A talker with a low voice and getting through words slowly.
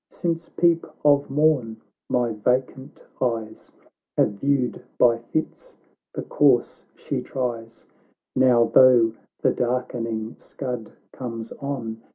Yes: low, 125 Hz; slow, 110 wpm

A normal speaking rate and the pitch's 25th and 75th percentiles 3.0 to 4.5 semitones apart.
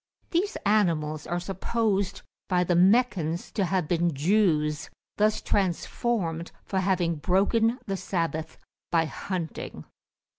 No: slow, 115 wpm; average, 3.8 semitones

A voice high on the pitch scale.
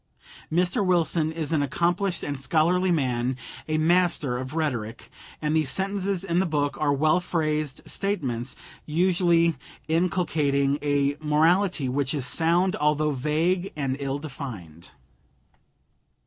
No: medium, 155 Hz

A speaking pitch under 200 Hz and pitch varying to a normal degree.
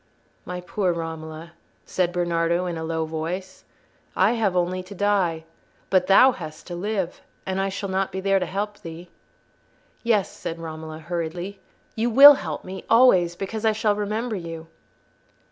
Yes: medium, 185 Hz; average, 3.4 semitones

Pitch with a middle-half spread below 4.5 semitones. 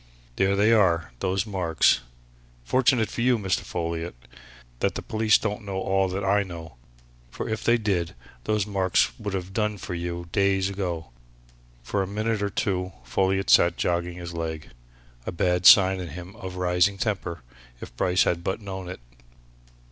Yes: average, 2.7 semitones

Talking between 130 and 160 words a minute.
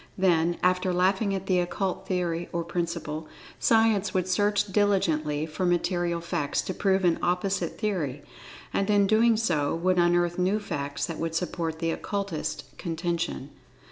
Yes: average, 155 wpm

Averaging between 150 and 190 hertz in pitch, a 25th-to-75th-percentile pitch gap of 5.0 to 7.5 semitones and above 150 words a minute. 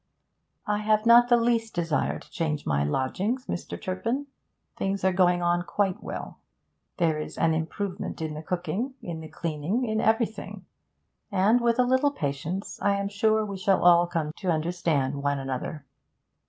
Yes: medium, 185 Hz; wide, 5.4 semitones; average, 165 wpm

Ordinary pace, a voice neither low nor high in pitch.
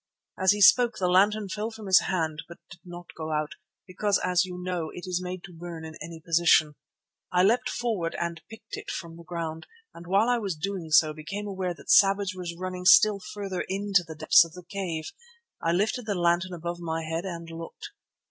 No: fast, 210 wpm; medium, 180 Hz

